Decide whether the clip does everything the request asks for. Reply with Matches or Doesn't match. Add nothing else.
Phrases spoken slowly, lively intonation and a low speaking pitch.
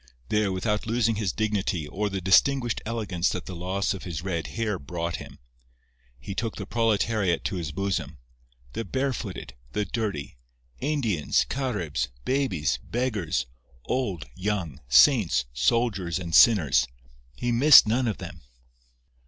Matches